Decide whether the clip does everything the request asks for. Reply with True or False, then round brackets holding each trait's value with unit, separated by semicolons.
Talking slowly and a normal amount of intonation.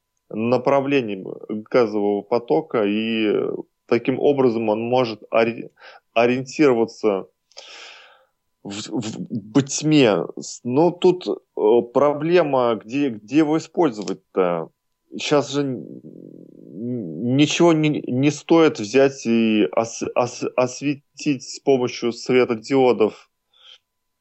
True (90 wpm; 4.1 semitones)